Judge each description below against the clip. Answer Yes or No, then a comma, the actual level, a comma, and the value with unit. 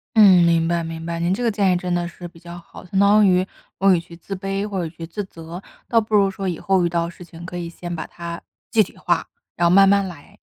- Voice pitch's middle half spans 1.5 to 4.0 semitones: Yes, narrow, 2.4 semitones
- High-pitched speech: No, medium, 175 Hz